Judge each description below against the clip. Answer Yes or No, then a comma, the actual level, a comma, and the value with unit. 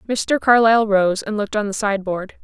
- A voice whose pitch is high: Yes, high, 210 Hz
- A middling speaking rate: No, fast, 220 wpm